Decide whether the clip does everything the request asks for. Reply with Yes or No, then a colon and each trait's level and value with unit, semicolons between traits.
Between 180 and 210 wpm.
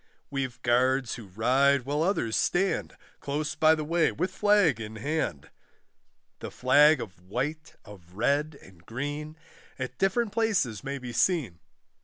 No: average, 145 wpm